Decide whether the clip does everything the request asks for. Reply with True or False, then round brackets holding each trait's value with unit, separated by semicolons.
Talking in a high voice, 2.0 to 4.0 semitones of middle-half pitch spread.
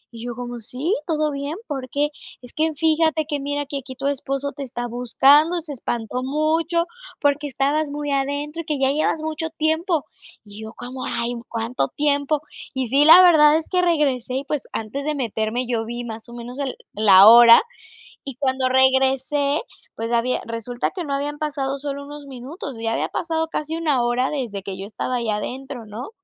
True (275 Hz; 3.7 semitones)